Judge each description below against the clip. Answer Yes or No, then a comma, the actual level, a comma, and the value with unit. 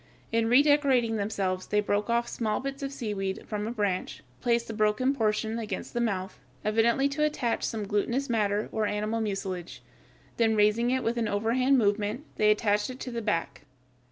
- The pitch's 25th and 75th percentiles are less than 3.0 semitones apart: Yes, narrow, 2.5 semitones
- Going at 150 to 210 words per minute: Yes, average, 180 wpm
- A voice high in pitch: Yes, high, 220 Hz